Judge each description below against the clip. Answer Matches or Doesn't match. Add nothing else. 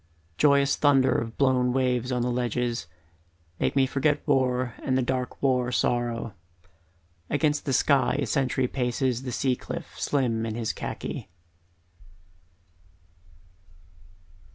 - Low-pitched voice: Matches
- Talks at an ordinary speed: Doesn't match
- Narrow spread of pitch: Matches